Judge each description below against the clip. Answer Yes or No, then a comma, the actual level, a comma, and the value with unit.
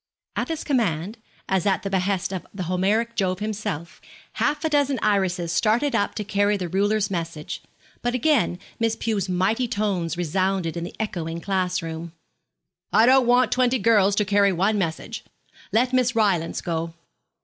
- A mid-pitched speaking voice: No, high, 200 Hz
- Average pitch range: Yes, average, 4.2 semitones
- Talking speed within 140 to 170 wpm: Yes, average, 165 wpm